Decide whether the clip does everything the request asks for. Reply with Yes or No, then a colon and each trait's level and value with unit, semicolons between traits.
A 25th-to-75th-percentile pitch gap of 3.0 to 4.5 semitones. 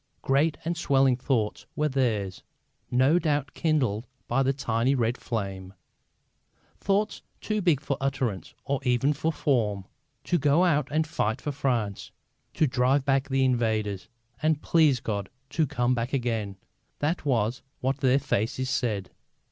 Yes: average, 4.1 semitones